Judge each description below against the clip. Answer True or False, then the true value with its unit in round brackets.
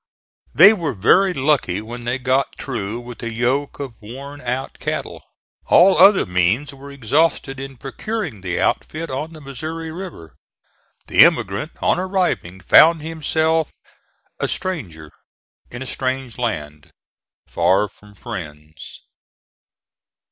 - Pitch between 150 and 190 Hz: False (130 Hz)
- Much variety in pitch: True (7.0 semitones)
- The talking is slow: True (125 wpm)